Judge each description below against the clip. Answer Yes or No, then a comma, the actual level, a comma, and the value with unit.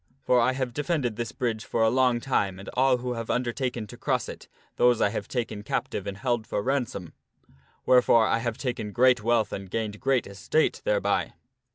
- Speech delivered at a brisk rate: No, average, 195 wpm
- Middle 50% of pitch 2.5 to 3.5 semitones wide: Yes, average, 2.8 semitones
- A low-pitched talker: Yes, low, 120 Hz